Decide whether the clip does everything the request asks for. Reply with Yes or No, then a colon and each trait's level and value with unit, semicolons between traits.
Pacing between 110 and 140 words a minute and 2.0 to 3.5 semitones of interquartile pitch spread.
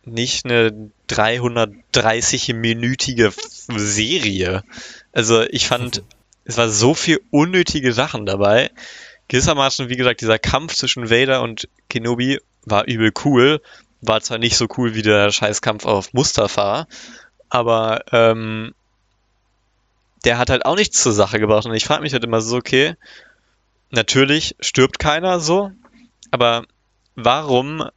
Yes: average, 130 wpm; average, 2.8 semitones